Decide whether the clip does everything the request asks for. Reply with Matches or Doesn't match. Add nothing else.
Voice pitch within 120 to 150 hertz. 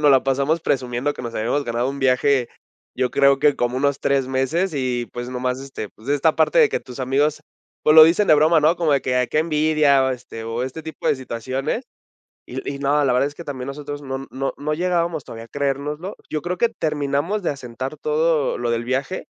Matches